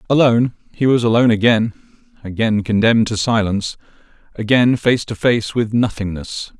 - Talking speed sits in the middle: No, slow, 110 wpm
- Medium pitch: No, low, 115 Hz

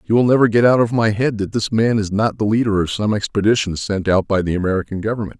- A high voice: No, low, 105 Hz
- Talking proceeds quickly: Yes, fast, 265 wpm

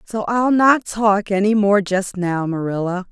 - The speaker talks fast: No, average, 175 wpm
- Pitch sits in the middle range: No, high, 200 Hz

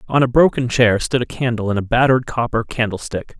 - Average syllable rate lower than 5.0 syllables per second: No, 5.9 syllables/s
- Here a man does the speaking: Yes, male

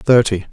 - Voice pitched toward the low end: Yes, low, 110 Hz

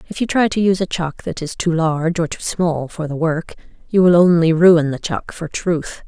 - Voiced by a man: No, female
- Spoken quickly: Yes, fast, 245 wpm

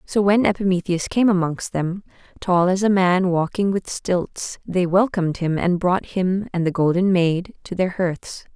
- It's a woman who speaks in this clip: Yes, female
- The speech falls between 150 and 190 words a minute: Yes, average, 180 wpm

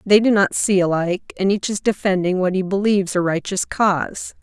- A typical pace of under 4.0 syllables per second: No, 5.5 syllables/s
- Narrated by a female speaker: Yes, female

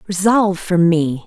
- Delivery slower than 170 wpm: Yes, average, 140 wpm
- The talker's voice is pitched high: No, medium, 180 Hz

